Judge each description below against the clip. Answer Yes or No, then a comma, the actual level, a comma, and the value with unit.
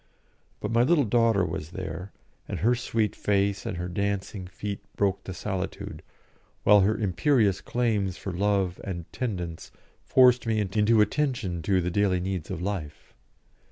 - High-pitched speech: No, low, 100 Hz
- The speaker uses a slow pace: No, average, 150 wpm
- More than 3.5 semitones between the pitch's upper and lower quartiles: No, average, 3.2 semitones